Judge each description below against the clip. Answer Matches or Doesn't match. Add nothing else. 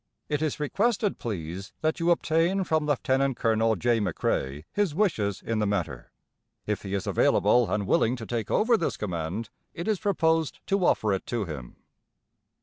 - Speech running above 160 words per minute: Matches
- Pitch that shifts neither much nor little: Doesn't match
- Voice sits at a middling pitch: Doesn't match